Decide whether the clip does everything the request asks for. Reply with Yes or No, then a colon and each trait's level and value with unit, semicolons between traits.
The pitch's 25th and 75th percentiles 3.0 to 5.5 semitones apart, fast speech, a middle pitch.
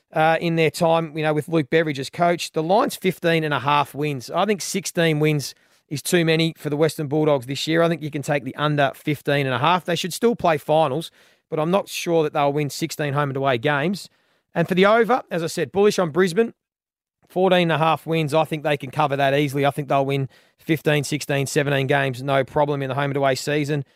No: narrow, 2.6 semitones; fast, 245 wpm; medium, 155 Hz